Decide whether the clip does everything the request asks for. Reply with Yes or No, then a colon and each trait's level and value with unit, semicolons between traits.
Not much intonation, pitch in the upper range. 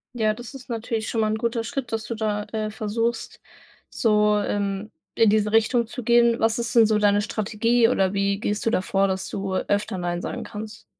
Yes: narrow, 1.9 semitones; high, 215 Hz